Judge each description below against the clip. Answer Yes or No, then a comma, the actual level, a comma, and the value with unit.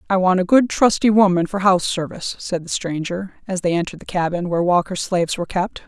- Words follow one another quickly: Yes, fast, 225 wpm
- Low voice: No, medium, 185 Hz